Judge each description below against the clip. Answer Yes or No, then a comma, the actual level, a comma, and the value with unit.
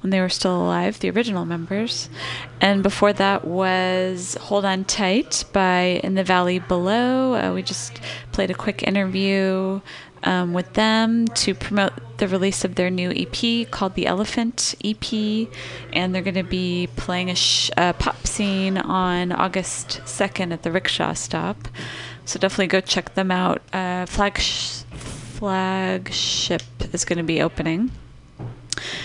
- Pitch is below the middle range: No, medium, 185 Hz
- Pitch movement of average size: No, narrow, 1.9 semitones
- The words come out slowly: No, average, 150 wpm